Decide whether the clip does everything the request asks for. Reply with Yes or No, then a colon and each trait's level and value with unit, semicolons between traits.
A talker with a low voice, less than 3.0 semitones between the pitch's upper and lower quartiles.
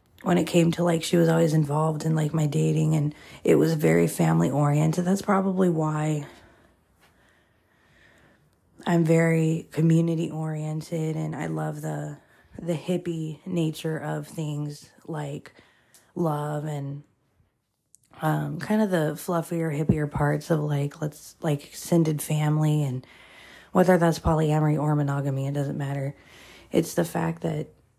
No: medium, 155 Hz; narrow, 2.5 semitones